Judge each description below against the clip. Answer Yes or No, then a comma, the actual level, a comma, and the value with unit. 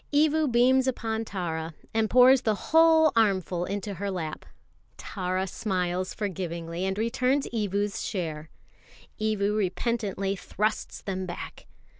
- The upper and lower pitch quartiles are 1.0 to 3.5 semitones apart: No, average, 4.1 semitones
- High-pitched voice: Yes, high, 205 Hz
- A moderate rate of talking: No, slow, 120 wpm